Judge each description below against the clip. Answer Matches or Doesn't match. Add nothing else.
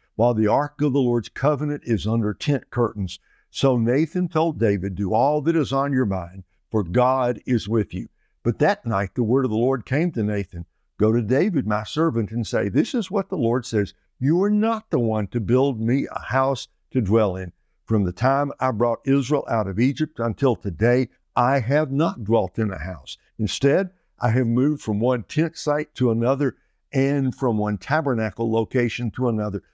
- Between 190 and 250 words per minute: Matches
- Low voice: Matches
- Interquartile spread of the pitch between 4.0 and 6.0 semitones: Matches